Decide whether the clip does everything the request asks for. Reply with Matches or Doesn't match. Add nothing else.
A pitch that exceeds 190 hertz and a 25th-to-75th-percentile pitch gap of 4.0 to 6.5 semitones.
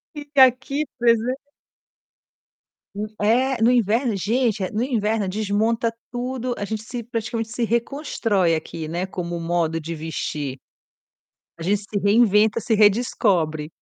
Matches